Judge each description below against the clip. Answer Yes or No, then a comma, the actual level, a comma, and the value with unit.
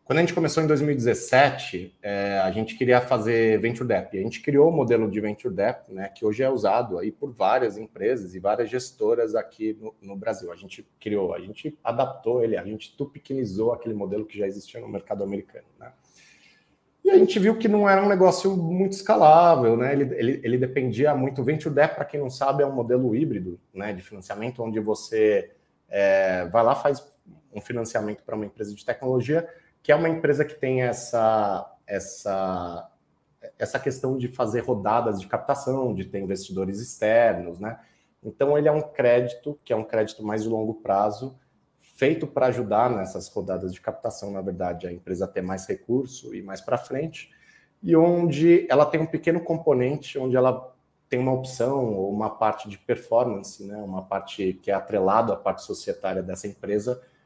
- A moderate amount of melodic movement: No, wide, 6.1 semitones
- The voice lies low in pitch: Yes, low, 125 Hz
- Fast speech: Yes, fast, 190 wpm